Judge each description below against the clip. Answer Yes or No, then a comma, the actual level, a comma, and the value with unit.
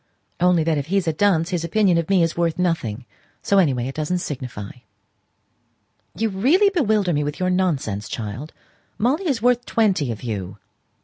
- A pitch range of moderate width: No, wide, 6.2 semitones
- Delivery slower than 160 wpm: No, average, 180 wpm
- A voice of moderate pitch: Yes, medium, 170 Hz